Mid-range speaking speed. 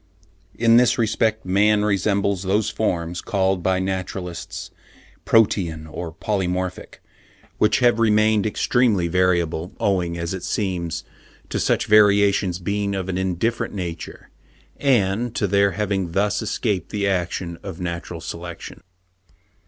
No: slow, 125 wpm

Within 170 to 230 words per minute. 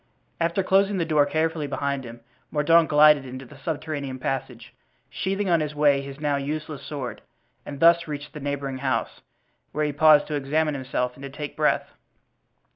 Yes: average, 175 wpm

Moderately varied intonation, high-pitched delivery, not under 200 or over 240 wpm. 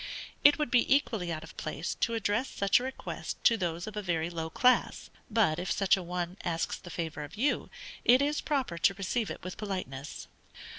No: wide, 5.7 semitones; high, 195 Hz; fast, 205 wpm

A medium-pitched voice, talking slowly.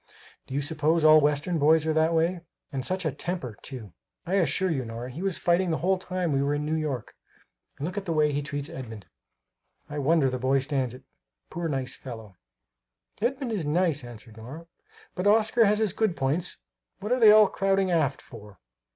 No: medium, 155 Hz; fast, 205 wpm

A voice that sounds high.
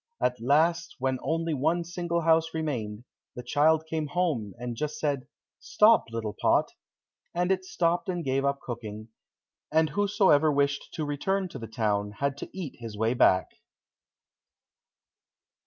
No: medium, 145 Hz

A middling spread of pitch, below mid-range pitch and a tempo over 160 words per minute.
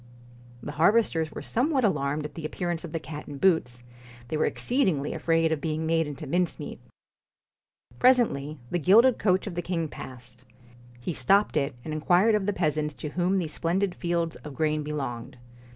No: average, 3.7 semitones; medium, 160 Hz; average, 180 wpm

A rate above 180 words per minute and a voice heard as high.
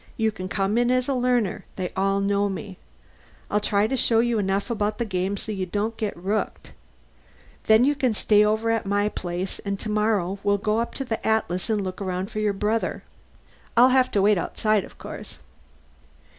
Yes: average, 200 wpm; high, 210 Hz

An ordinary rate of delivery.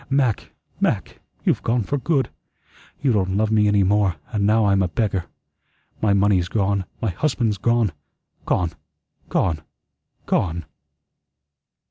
No: slow, 130 wpm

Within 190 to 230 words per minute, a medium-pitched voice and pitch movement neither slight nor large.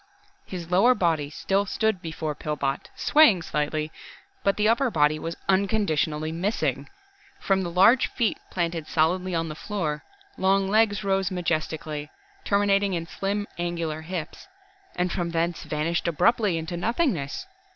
No: average, 140 wpm; medium, 175 Hz; average, 4.0 semitones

